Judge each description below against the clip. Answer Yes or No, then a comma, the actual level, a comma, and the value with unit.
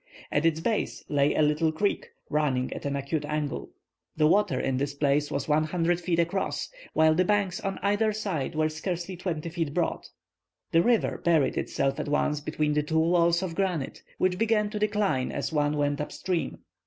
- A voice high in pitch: No, medium, 160 Hz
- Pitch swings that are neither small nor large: Yes, average, 3.7 semitones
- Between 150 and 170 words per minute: No, average, 190 wpm